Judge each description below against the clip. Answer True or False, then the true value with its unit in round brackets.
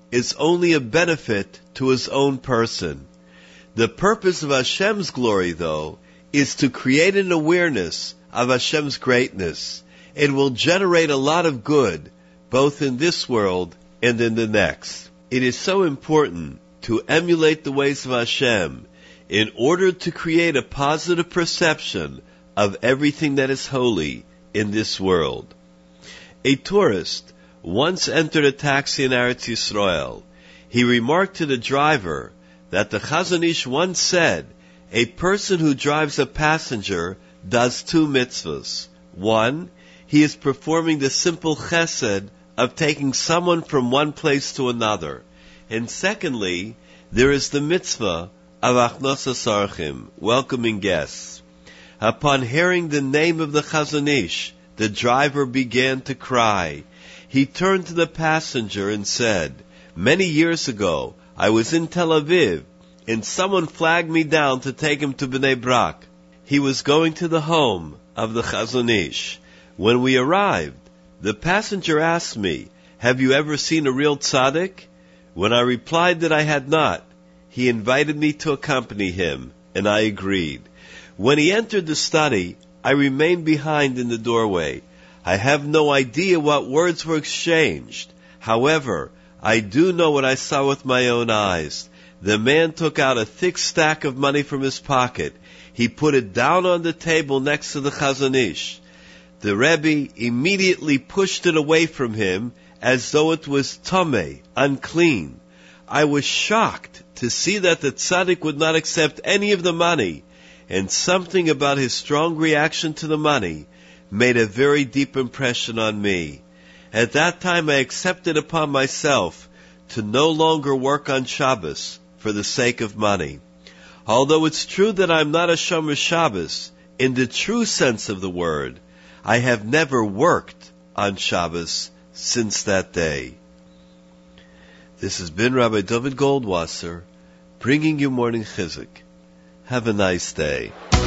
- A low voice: True (130 Hz)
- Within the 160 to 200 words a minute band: False (150 wpm)